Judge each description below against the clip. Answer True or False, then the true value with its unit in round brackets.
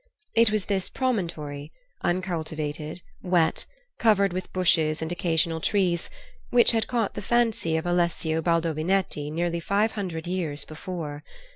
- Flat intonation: False (3.4 semitones)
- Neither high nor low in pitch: True (175 Hz)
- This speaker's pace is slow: True (130 wpm)